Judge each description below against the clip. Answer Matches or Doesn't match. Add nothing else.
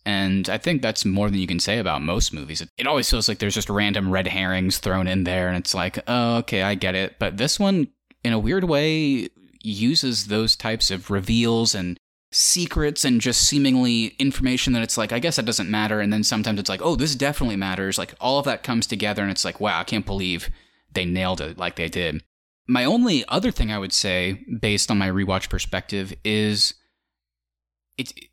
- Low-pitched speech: Matches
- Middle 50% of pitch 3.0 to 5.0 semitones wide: Matches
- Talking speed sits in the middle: Doesn't match